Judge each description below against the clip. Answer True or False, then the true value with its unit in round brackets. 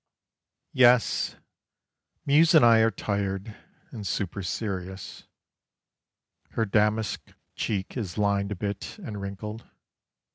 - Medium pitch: False (105 Hz)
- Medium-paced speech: False (105 wpm)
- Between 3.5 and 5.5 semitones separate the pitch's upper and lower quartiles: False (2.5 semitones)